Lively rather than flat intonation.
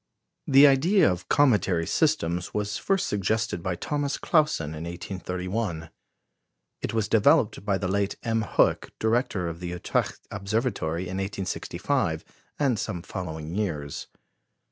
No: average, 4.5 semitones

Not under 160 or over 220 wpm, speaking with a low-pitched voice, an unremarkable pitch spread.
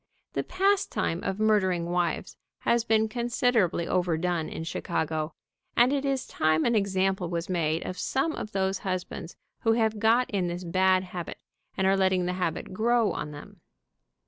No: average, 170 wpm; high, 190 Hz; average, 4.3 semitones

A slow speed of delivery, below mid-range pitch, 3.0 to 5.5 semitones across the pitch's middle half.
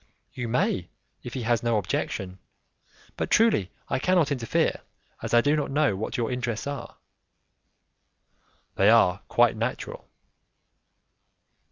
Yes: slow, 130 wpm; low, 120 Hz; average, 3.9 semitones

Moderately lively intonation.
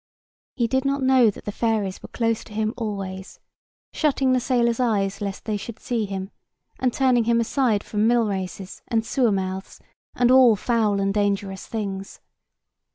Yes: average, 3.4 semitones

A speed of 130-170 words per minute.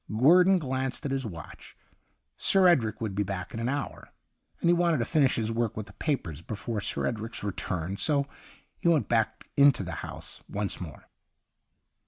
No: average, 180 wpm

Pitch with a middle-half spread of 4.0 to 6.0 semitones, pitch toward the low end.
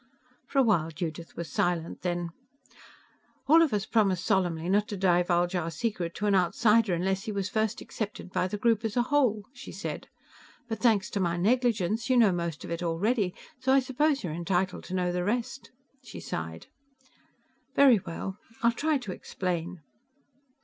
No: average, 4.8 semitones; high, 195 Hz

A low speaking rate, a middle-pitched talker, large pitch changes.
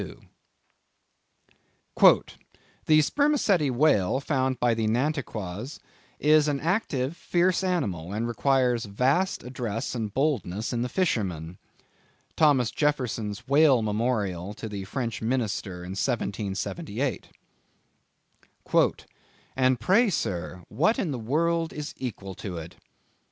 No: slow, 110 wpm; low, 125 Hz; wide, 6.4 semitones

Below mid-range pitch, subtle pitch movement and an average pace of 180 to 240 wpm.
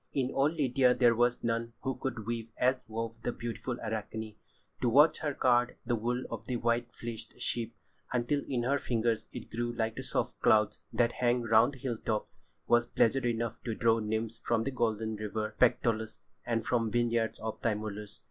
Yes: low, 115 Hz; narrow, 1.7 semitones; average, 190 wpm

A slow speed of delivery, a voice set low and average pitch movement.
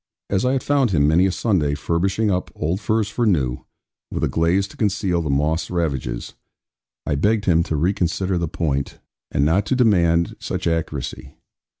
No: average, 180 wpm; very low, 85 Hz; average, 4.3 semitones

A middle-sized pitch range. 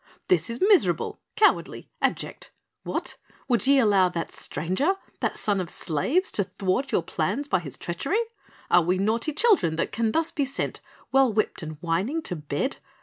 No: wide, 8.2 semitones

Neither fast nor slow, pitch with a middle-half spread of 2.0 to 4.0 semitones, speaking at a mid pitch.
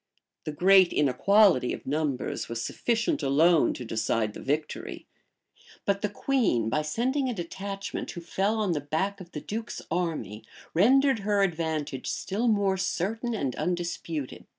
No: average, 150 wpm; wide, 5.6 semitones; medium, 175 Hz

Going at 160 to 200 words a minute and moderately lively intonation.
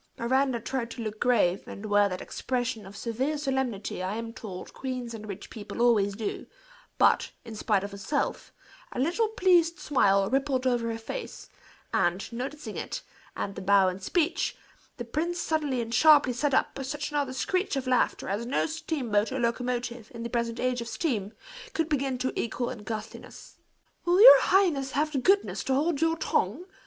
Yes: average, 180 wpm; average, 5.0 semitones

